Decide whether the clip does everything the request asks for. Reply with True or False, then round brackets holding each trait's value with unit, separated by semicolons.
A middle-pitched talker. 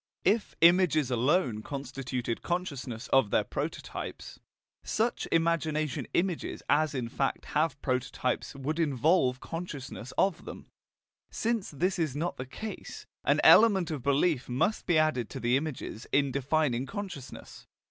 True (145 Hz)